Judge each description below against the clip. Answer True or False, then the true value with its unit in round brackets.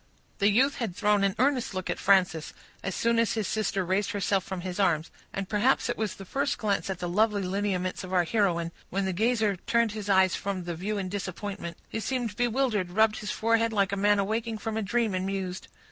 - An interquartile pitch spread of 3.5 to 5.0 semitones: False (2.9 semitones)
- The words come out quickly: True (220 wpm)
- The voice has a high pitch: True (200 Hz)